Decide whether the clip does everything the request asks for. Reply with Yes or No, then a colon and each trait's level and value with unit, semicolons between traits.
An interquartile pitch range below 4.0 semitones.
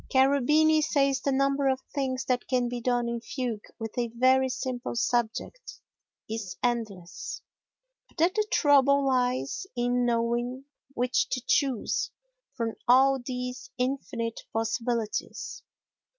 Yes: narrow, 2.5 semitones